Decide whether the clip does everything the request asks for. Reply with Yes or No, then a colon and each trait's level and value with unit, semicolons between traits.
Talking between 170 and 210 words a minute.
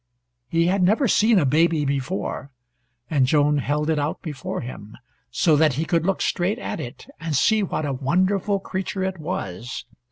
Yes: average, 180 wpm